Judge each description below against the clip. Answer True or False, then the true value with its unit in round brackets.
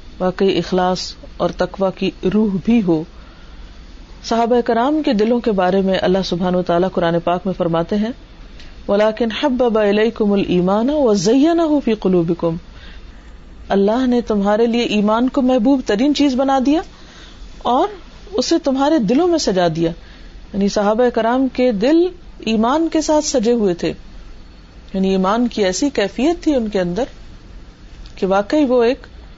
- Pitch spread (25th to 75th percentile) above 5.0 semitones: True (5.6 semitones)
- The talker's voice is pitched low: False (220 Hz)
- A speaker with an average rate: True (135 wpm)